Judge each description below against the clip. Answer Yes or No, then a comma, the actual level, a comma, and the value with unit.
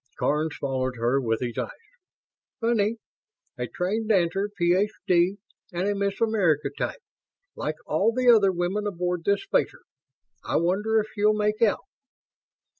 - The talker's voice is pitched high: Yes, high, 195 Hz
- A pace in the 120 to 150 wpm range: Yes, average, 140 wpm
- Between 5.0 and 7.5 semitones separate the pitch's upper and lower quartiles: No, average, 3.9 semitones